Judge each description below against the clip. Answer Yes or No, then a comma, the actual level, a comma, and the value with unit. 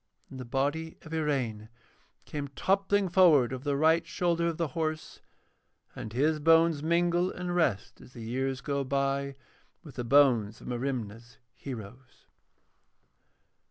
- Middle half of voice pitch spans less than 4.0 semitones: No, average, 4.4 semitones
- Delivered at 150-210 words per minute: No, average, 140 wpm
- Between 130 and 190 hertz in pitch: Yes, medium, 140 Hz